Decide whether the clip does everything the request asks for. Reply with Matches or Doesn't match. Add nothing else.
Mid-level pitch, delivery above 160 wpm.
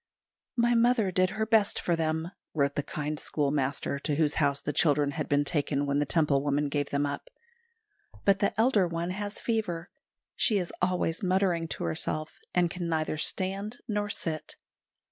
Matches